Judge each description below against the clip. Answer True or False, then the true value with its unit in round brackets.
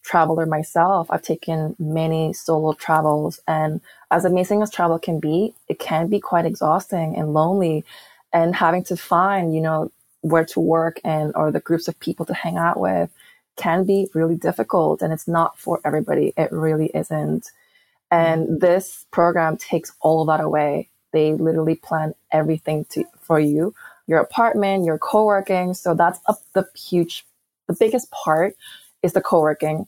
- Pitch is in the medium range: True (165 Hz)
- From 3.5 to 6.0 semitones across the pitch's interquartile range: False (2.4 semitones)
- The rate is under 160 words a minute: False (165 wpm)